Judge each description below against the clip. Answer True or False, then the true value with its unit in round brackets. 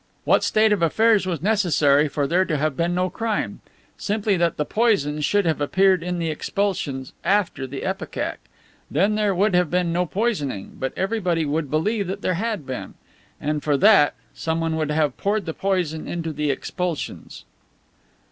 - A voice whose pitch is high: False (175 Hz)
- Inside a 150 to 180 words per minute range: True (170 wpm)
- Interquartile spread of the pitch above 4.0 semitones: True (4.8 semitones)